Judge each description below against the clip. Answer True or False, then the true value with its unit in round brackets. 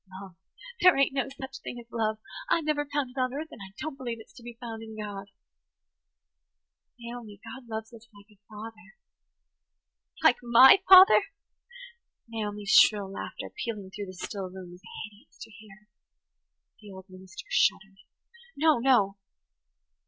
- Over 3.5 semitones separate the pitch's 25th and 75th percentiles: True (3.9 semitones)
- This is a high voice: True (220 Hz)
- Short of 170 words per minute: True (160 wpm)